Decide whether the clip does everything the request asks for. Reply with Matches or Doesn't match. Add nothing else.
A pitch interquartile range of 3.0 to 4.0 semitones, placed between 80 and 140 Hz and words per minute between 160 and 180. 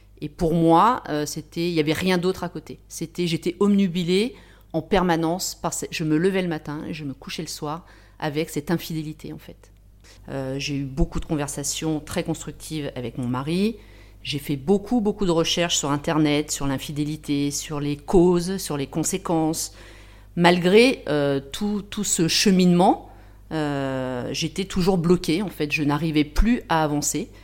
Doesn't match